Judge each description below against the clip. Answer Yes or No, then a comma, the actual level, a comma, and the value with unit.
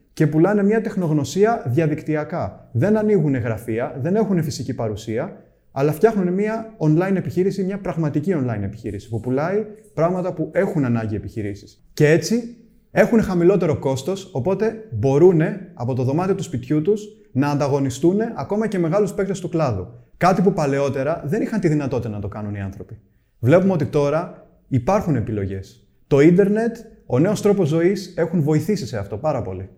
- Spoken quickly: No, average, 155 wpm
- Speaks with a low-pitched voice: No, medium, 160 Hz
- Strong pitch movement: Yes, wide, 6.9 semitones